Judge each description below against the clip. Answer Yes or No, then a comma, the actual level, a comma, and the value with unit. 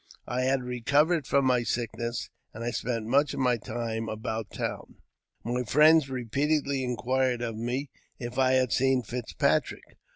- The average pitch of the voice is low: Yes, low, 125 Hz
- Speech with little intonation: Yes, narrow, 2.2 semitones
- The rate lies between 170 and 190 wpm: No, average, 155 wpm